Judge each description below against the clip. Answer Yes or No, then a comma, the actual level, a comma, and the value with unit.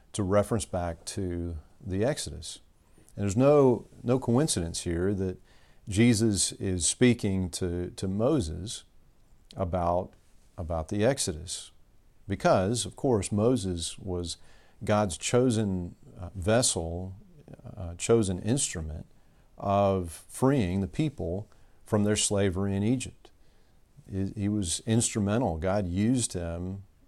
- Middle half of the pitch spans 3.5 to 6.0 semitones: Yes, average, 4.4 semitones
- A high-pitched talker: No, low, 100 Hz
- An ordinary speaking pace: No, slow, 110 wpm